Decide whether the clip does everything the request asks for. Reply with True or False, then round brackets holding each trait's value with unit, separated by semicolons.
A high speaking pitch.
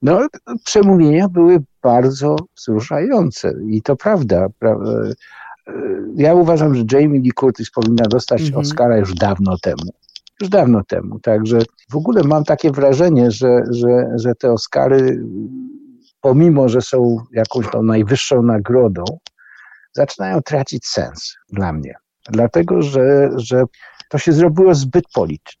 False (130 Hz)